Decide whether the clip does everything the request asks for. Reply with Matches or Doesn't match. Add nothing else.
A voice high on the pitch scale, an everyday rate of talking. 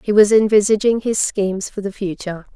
Matches